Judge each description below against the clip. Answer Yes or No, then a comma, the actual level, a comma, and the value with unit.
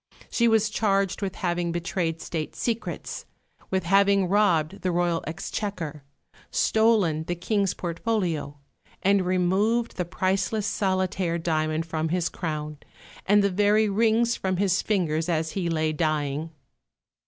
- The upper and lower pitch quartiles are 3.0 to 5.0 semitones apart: Yes, average, 3.6 semitones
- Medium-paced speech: No, slow, 130 wpm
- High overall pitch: No, medium, 180 Hz